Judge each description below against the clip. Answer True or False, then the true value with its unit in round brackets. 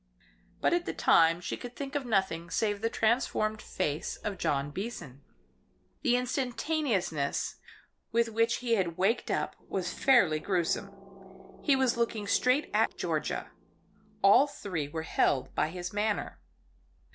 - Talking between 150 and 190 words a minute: False (140 wpm)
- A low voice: False (210 Hz)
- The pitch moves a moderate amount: False (6.2 semitones)